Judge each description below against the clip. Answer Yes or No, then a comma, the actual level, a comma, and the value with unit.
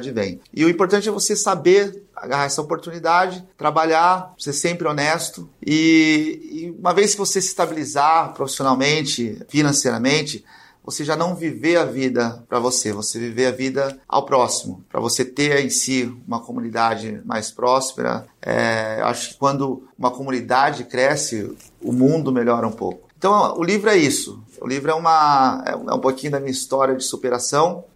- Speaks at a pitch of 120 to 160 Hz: Yes, medium, 140 Hz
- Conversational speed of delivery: Yes, average, 170 wpm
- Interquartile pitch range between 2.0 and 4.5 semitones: No, average, 5.1 semitones